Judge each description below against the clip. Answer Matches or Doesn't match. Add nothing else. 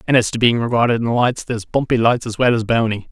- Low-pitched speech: Matches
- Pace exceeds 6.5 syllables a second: Doesn't match